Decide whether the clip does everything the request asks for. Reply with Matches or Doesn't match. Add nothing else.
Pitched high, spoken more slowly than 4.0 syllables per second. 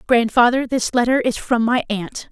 Doesn't match